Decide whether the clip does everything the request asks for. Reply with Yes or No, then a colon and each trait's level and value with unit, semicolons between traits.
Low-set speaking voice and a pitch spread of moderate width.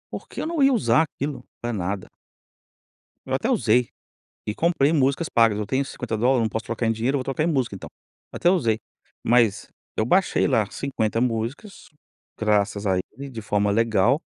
Yes: low, 120 Hz; average, 4.3 semitones